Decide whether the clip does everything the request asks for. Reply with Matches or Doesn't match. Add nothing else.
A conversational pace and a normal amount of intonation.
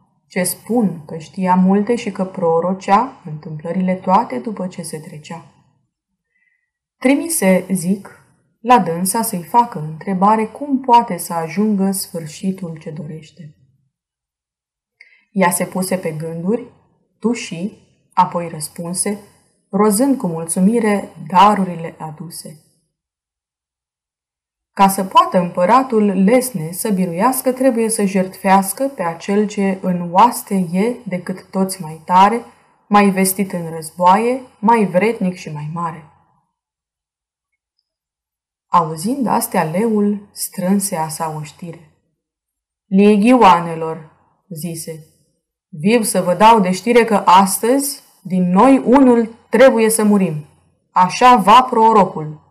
Doesn't match